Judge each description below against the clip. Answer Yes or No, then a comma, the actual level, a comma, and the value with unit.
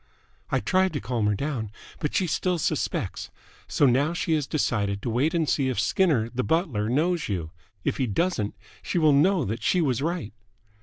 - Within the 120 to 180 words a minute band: No, average, 195 wpm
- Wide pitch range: Yes, wide, 6.8 semitones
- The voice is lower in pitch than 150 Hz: Yes, medium, 140 Hz